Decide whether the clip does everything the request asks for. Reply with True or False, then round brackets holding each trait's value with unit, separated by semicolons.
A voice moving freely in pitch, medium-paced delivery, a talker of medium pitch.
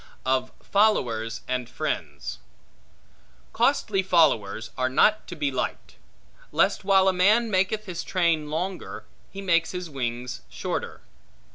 False (6.9 semitones; 125 wpm; 170 Hz)